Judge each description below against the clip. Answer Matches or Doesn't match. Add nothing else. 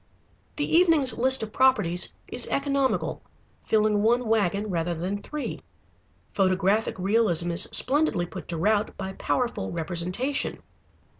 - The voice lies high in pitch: Matches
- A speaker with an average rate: Doesn't match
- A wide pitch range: Matches